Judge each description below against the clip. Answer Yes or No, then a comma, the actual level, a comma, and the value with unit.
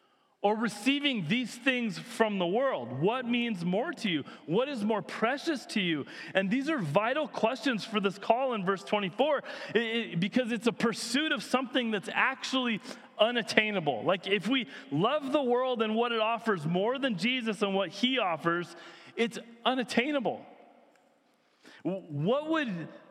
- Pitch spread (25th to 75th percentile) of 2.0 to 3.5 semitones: No, average, 4.1 semitones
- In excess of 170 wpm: No, average, 155 wpm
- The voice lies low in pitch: No, high, 230 Hz